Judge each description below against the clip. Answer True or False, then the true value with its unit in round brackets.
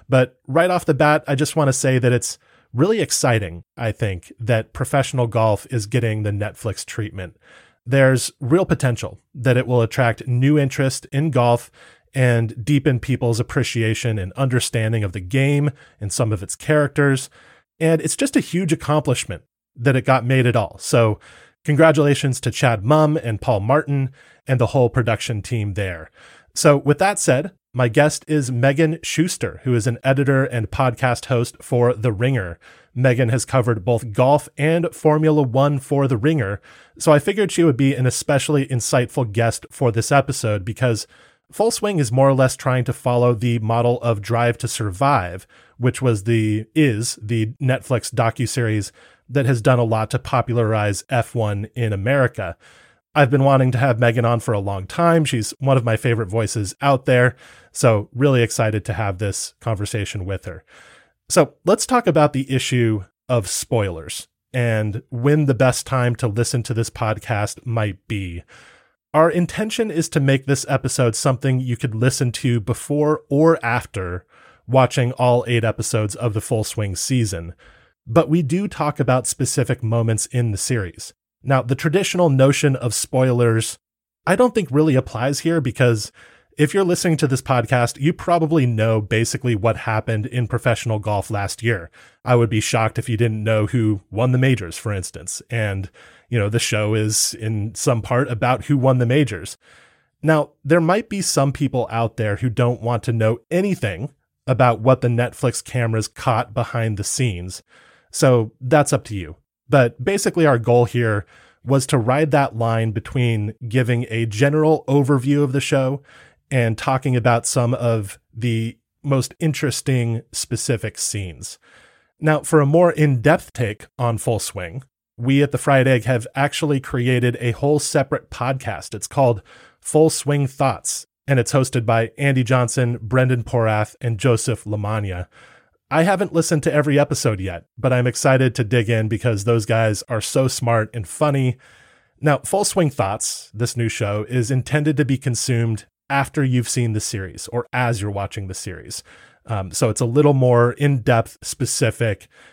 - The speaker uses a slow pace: False (170 wpm)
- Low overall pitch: True (125 Hz)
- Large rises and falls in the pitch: False (3.8 semitones)